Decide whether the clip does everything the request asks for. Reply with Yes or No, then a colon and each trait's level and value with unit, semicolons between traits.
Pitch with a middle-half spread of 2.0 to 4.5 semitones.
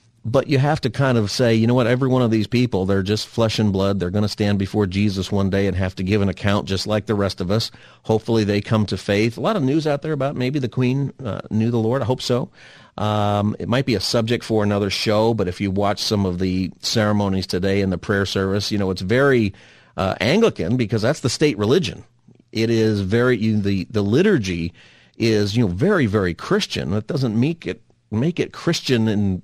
Yes: average, 3.8 semitones